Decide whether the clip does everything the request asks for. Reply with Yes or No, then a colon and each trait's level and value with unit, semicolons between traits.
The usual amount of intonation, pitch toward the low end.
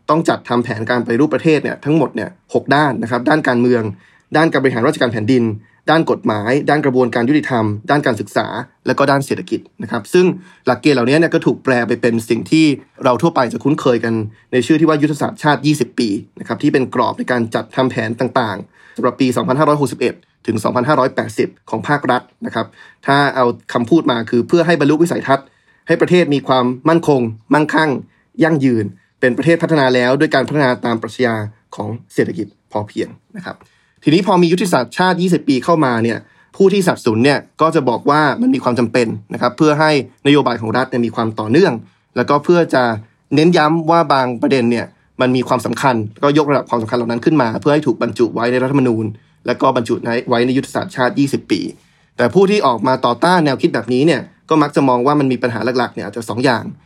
Yes: average, 4.2 semitones; low, 130 Hz